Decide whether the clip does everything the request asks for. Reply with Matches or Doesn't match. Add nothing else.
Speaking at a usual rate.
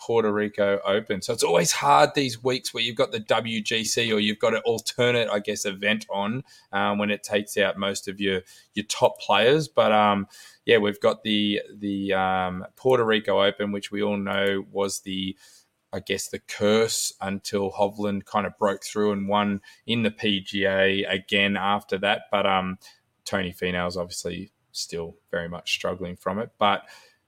Matches